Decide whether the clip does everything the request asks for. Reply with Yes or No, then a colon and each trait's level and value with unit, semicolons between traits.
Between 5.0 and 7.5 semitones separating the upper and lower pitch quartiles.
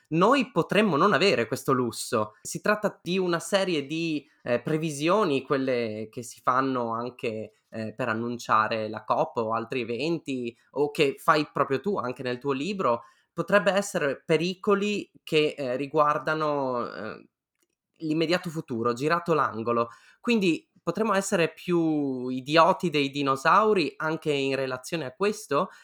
Yes: average, 5.3 semitones